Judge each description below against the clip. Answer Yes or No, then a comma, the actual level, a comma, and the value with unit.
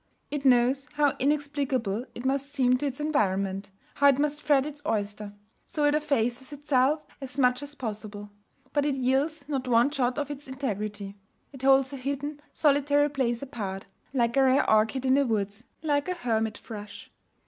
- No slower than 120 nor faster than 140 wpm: No, average, 175 wpm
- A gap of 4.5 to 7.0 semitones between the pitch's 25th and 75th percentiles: No, average, 3.9 semitones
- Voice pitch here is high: Yes, very high, 265 Hz